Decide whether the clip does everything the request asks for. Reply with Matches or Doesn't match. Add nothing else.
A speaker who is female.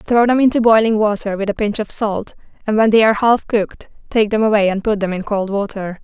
Matches